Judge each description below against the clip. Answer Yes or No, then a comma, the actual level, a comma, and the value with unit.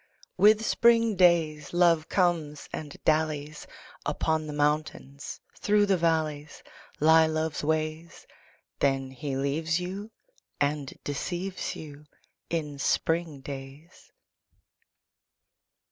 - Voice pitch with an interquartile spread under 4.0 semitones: Yes, average, 2.9 semitones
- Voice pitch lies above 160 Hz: No, medium, 155 Hz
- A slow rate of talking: Yes, slow, 100 wpm